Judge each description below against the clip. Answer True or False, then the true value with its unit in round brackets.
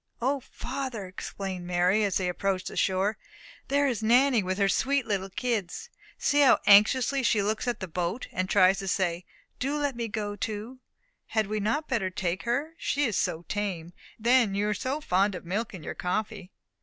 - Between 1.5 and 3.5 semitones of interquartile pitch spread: False (4.9 semitones)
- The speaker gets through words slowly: False (195 wpm)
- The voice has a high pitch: True (210 Hz)